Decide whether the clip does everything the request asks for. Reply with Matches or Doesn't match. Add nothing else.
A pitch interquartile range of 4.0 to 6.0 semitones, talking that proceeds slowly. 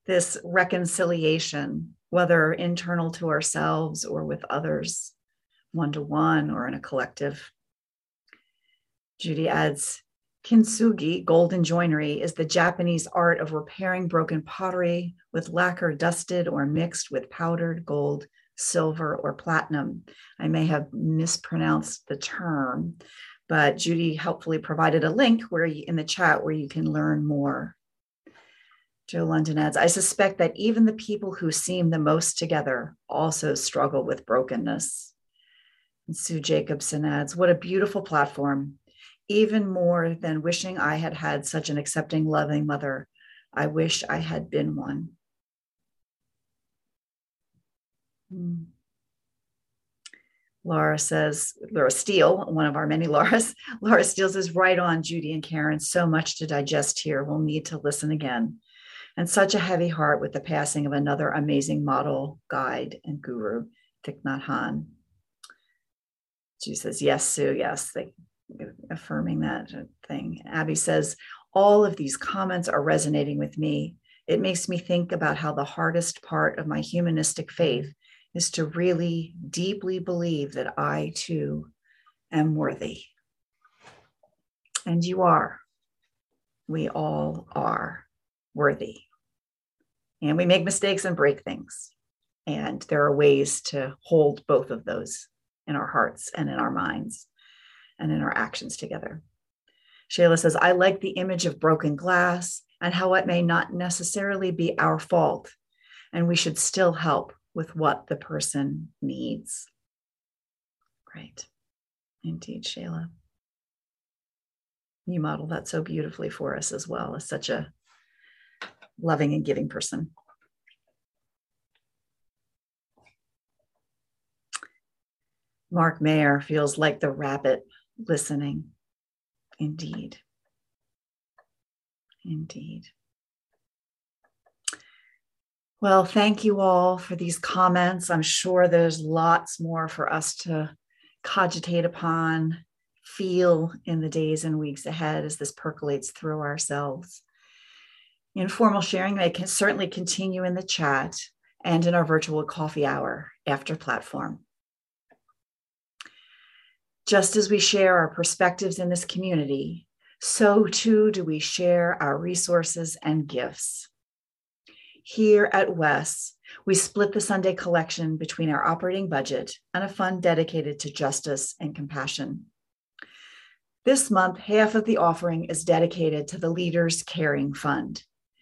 Doesn't match